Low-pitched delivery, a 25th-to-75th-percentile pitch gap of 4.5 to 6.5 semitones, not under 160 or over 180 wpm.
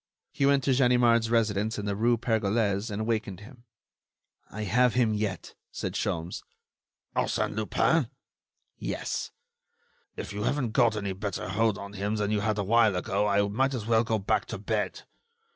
No: low, 110 Hz; narrow, 2.6 semitones; average, 170 wpm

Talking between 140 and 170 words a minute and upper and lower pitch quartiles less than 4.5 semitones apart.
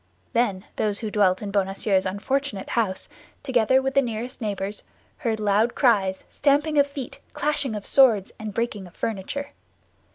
No: average, 155 wpm; average, 4.9 semitones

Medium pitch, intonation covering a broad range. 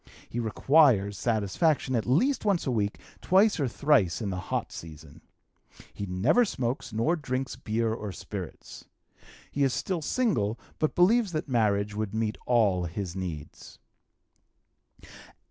No: low, 115 Hz; wide, 7.0 semitones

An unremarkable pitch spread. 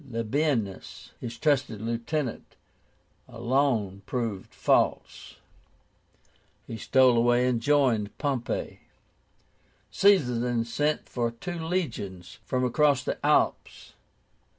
Yes: average, 3.8 semitones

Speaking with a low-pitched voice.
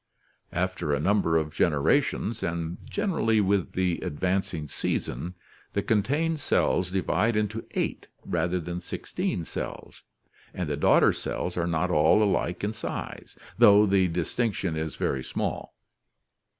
Yes: very low, 90 Hz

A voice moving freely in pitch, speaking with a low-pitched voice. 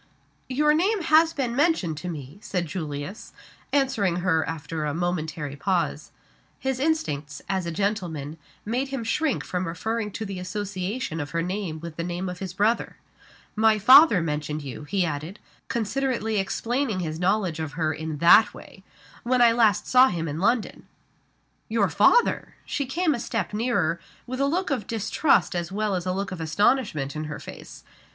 No: wide, 6.6 semitones; high, 195 Hz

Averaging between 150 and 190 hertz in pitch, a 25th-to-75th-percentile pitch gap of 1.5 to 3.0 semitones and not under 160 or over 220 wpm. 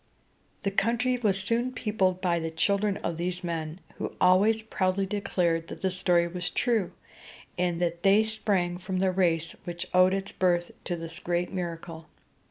Yes: medium, 185 Hz; narrow, 2.6 semitones; average, 170 wpm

